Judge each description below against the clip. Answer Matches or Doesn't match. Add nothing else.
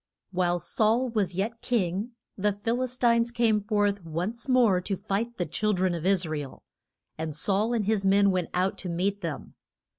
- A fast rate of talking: Doesn't match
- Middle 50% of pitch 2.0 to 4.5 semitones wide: Matches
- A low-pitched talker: Doesn't match